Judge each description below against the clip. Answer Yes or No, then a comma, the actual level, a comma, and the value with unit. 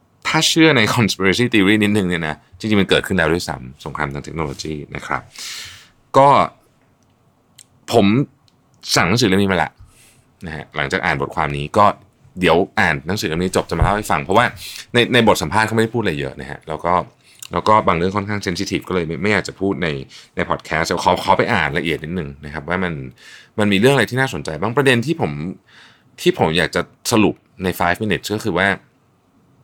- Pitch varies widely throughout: Yes, wide, 5.7 semitones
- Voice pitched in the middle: No, very low, 95 Hz